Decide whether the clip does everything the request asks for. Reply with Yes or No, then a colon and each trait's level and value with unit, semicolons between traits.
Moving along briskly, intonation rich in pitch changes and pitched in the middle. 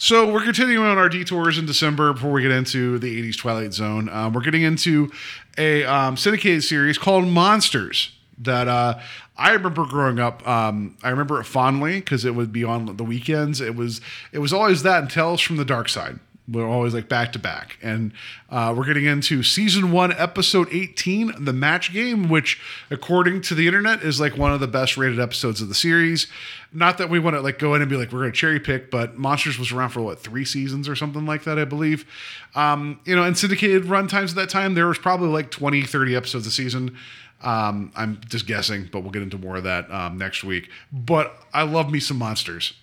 Yes: fast, 225 wpm; wide, 5.8 semitones; medium, 145 Hz